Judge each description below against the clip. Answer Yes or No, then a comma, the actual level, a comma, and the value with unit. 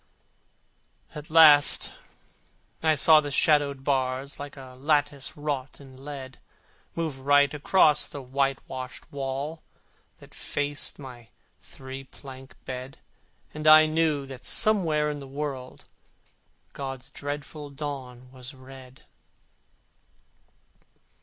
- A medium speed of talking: No, slow, 105 wpm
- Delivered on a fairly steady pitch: Yes, narrow, 2.0 semitones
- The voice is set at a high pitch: No, medium, 140 Hz